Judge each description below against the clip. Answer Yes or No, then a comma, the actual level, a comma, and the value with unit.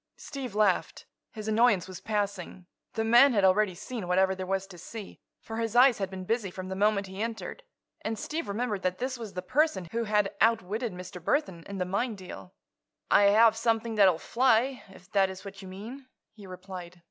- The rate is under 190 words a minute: No, fast, 205 wpm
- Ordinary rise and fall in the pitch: Yes, average, 3.3 semitones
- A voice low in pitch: No, high, 205 Hz